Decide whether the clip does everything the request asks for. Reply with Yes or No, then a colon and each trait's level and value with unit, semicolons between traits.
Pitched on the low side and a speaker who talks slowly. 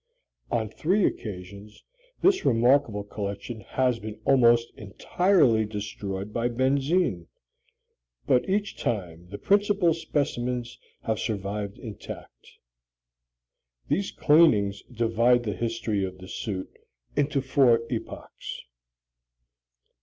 Yes: low, 115 Hz; slow, 100 wpm